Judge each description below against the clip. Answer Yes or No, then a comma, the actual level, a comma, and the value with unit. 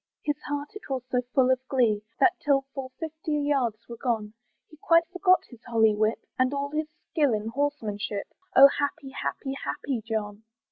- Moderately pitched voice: No, very high, 265 Hz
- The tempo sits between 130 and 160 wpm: No, average, 180 wpm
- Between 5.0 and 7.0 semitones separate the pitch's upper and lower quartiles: No, average, 4.5 semitones